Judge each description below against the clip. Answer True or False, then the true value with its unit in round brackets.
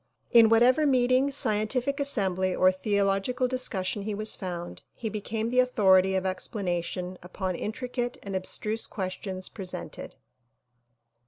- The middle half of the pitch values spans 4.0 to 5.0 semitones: True (4.6 semitones)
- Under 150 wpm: True (135 wpm)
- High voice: True (210 Hz)